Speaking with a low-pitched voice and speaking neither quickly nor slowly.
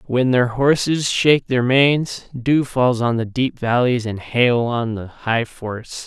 Yes: low, 125 Hz; average, 180 wpm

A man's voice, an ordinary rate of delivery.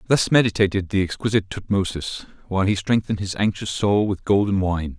Yes: male; average, 170 wpm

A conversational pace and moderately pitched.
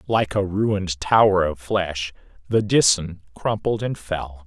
No: average, 150 wpm; very low, 95 Hz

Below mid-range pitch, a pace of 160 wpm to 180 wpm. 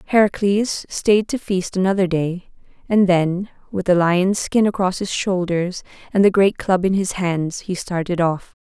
No: high, 190 Hz; average, 175 wpm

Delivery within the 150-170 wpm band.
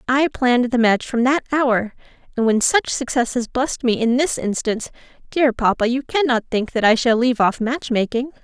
No: fast, 205 wpm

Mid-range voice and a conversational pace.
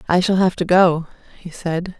No: medium, 175 Hz; fast, 210 wpm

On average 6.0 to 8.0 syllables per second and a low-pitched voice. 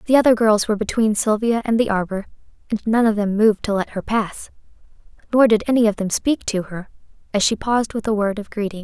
No: 6.2 syllables/s; high, 215 Hz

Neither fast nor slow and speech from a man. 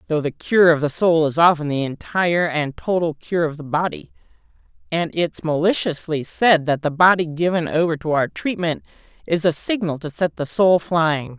No: average, 190 wpm; female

